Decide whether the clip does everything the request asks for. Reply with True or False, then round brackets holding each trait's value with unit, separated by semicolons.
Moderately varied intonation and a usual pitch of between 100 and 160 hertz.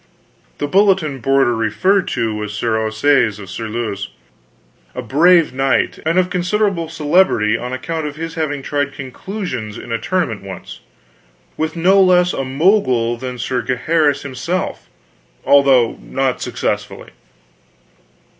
False (6.2 semitones; 140 Hz)